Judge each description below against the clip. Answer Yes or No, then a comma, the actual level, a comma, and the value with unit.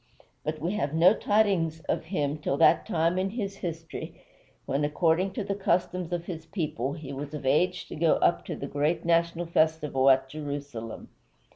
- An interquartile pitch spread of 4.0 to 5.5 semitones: No, average, 3.4 semitones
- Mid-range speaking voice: Yes, medium, 160 Hz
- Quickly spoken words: No, average, 180 wpm